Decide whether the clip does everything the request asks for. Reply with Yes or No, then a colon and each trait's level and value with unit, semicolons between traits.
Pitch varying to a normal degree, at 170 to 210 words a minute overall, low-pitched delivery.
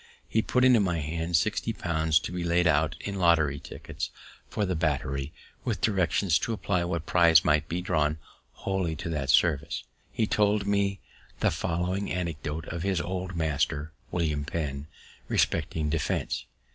No: average, 3.3 semitones; average, 160 wpm; very low, 85 Hz